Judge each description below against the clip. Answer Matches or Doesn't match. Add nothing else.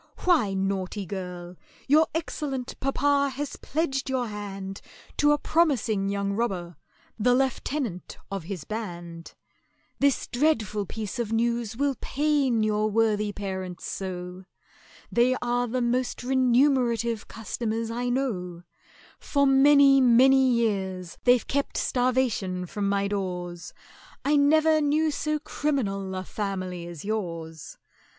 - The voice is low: Doesn't match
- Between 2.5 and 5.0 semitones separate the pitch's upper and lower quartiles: Doesn't match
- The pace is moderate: Doesn't match